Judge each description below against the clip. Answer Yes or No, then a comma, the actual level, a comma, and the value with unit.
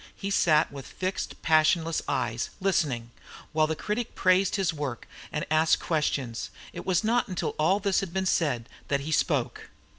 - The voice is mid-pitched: Yes, medium, 160 Hz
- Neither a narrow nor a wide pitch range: Yes, average, 4.4 semitones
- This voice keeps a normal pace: Yes, average, 170 wpm